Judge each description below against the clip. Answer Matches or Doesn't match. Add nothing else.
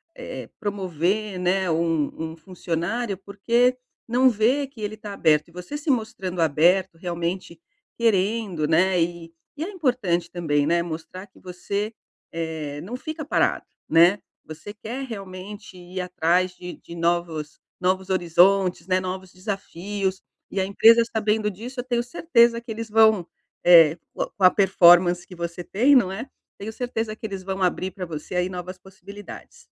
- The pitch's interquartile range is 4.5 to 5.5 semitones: Doesn't match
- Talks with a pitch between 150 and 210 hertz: Matches